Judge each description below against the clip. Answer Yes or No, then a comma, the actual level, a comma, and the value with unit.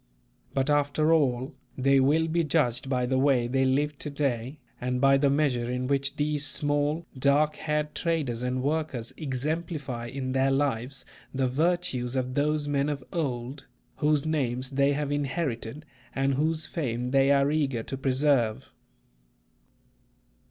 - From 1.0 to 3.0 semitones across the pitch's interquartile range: Yes, narrow, 2.6 semitones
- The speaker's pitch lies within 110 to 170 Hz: Yes, medium, 140 Hz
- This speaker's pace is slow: No, average, 150 wpm